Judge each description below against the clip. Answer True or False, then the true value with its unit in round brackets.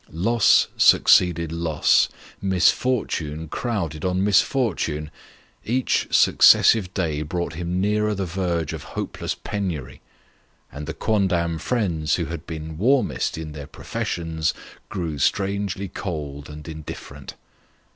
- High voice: False (85 Hz)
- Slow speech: True (115 wpm)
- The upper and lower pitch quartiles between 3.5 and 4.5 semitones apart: True (4.1 semitones)